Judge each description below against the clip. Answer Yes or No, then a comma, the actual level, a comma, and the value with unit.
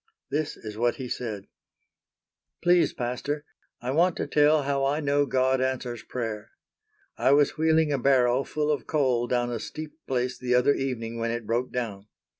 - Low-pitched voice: Yes, low, 130 Hz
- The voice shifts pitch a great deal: No, average, 3.2 semitones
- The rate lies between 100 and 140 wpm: No, average, 175 wpm